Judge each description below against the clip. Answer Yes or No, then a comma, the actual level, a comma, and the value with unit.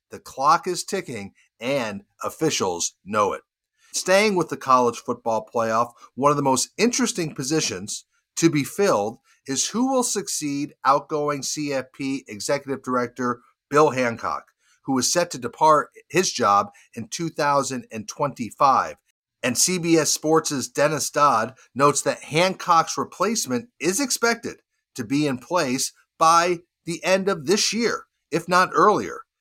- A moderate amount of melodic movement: No, wide, 6.1 semitones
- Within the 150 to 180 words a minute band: No, slow, 135 wpm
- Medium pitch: Yes, medium, 155 Hz